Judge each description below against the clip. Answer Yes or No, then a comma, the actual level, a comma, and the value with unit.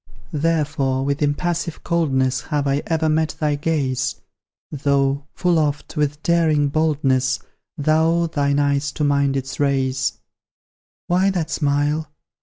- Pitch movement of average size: No, narrow, 2.3 semitones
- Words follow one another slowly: Yes, slow, 125 wpm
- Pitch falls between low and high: Yes, medium, 145 Hz